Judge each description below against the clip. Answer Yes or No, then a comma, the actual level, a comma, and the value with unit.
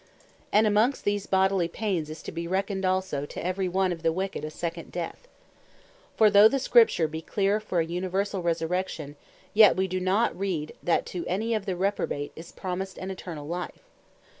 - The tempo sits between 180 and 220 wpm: Yes, average, 190 wpm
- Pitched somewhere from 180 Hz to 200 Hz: Yes, medium, 185 Hz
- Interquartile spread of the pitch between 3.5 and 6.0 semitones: No, average, 2.8 semitones